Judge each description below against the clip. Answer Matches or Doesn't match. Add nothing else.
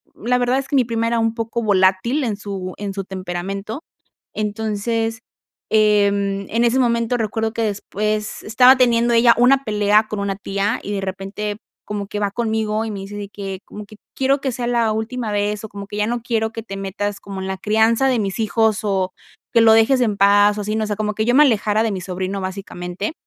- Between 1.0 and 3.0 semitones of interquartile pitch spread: Matches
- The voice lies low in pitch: Doesn't match